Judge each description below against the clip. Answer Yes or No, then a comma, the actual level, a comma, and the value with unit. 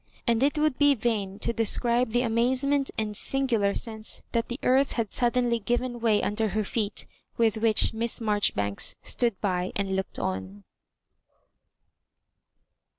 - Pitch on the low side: No, high, 230 Hz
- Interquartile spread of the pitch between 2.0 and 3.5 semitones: Yes, average, 2.9 semitones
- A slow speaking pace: No, average, 145 wpm